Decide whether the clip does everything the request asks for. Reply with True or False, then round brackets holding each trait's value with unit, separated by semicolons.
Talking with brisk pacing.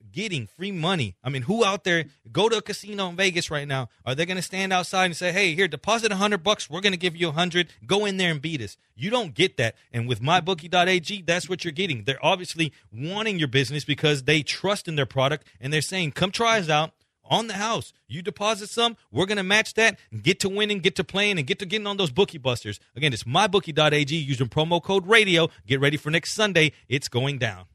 True (235 wpm)